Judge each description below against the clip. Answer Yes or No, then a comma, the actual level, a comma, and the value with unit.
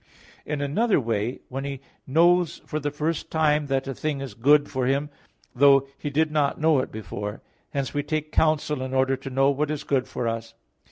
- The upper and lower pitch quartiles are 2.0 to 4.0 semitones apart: Yes, narrow, 2.4 semitones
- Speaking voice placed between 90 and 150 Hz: Yes, medium, 140 Hz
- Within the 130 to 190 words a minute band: No, fast, 205 wpm